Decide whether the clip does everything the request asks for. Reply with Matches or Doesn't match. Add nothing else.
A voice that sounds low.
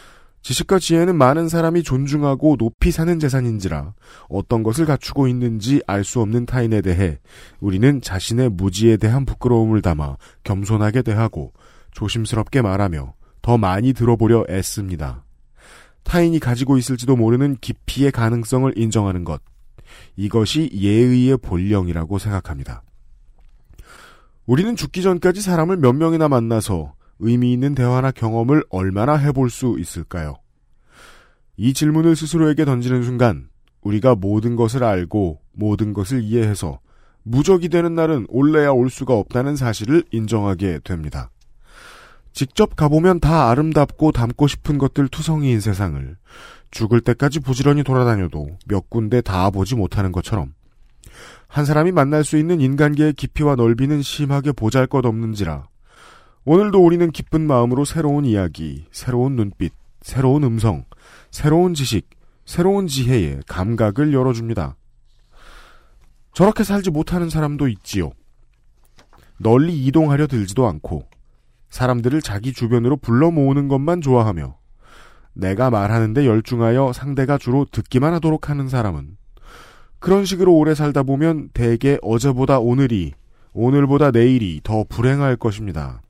Matches